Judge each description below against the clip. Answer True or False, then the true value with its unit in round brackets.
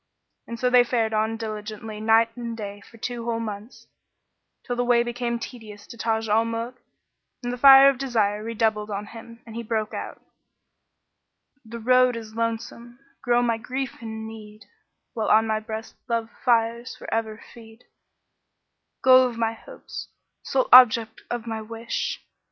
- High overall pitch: True (230 Hz)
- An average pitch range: False (1.5 semitones)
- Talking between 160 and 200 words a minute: True (165 wpm)